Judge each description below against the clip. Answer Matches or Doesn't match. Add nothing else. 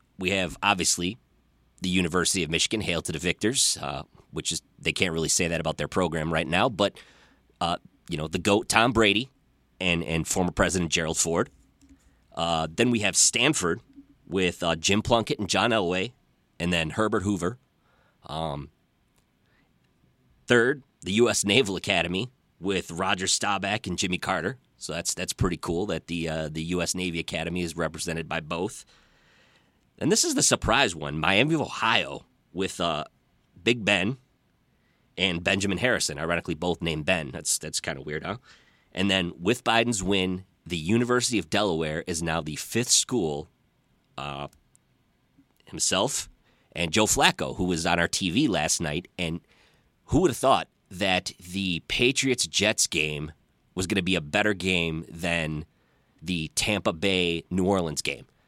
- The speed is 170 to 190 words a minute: Doesn't match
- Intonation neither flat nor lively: Matches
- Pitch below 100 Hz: Matches